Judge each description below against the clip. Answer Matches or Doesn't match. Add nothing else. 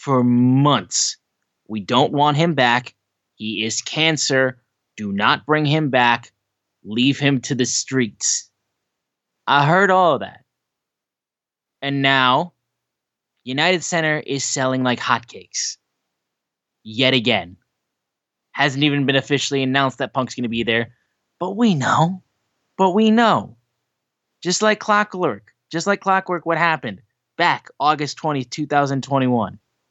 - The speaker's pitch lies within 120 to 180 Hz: Matches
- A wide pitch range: Doesn't match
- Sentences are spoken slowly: Matches